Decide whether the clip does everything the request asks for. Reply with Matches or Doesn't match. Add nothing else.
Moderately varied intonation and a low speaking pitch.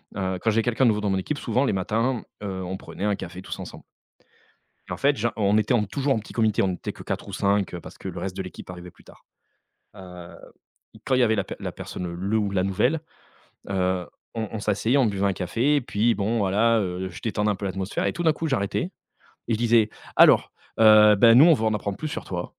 Matches